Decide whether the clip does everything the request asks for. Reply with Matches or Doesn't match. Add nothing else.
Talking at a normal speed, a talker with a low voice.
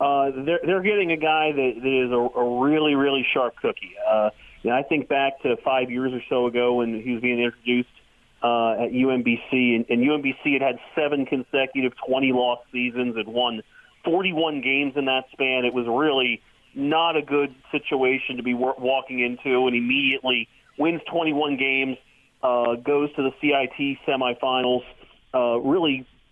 Matches